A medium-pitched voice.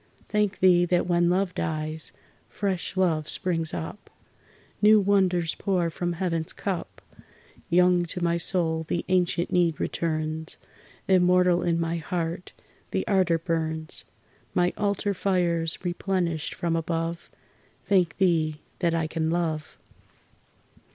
Yes: medium, 175 Hz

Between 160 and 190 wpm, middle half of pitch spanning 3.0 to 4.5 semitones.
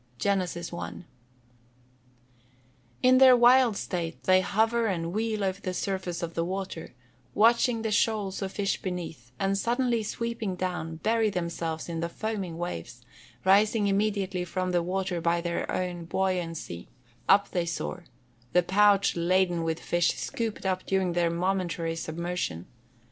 No: average, 145 wpm; average, 3.4 semitones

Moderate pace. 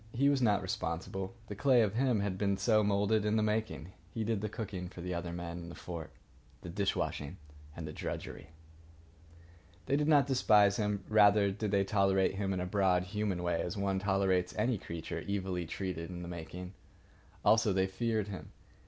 Yes: average, 195 wpm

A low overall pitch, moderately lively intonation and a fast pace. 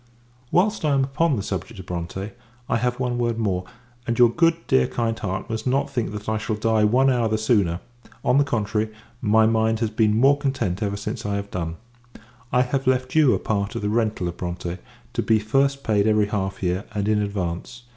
Yes: low, 110 Hz; average, 3.6 semitones; fast, 215 wpm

